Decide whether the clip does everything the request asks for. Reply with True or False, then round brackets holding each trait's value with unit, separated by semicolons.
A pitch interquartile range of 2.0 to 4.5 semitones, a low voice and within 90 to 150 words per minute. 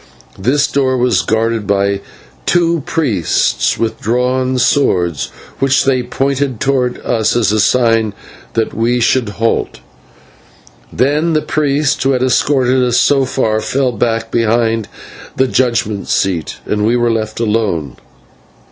True (3.3 semitones; 120 Hz; 135 wpm)